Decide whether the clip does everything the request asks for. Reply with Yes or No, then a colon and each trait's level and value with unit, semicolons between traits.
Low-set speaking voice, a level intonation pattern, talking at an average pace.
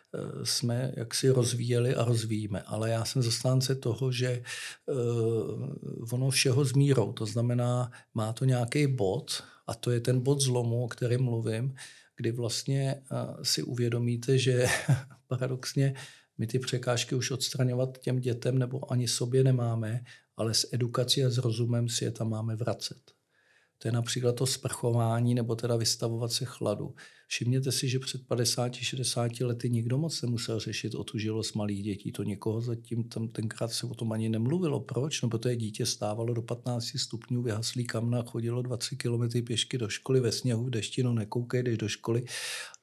Yes: low, 120 Hz; narrow, 1.9 semitones; average, 160 wpm